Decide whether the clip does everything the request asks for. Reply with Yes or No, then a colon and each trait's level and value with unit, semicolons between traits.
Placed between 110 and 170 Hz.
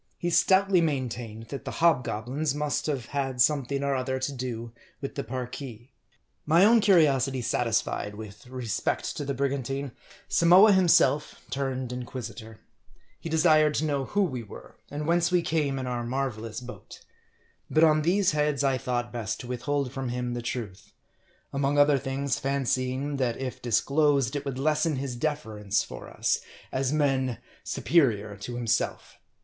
Yes: low, 135 Hz